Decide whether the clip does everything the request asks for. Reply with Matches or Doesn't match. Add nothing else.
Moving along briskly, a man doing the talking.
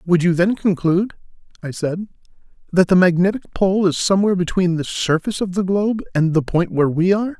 Doesn't match